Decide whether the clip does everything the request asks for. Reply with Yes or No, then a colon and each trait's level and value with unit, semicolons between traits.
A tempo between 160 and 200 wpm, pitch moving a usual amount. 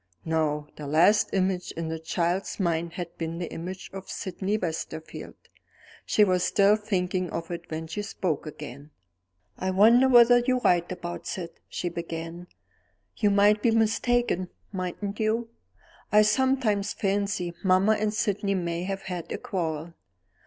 No: average, 150 wpm; average, 3.7 semitones